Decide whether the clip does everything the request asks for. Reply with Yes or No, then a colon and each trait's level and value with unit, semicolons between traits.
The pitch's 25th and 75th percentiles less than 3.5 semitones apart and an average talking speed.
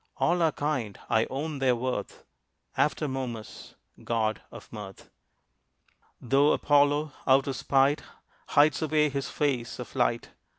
No: average, 3.1 semitones; slow, 130 wpm